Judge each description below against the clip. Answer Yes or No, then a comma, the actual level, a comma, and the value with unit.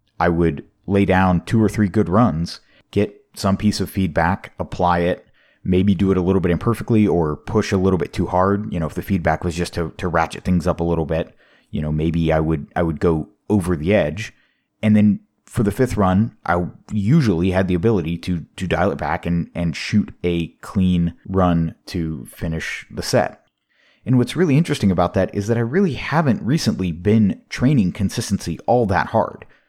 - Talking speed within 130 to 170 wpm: No, average, 200 wpm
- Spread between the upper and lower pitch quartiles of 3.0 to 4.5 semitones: Yes, average, 3.6 semitones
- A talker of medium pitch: No, very low, 95 Hz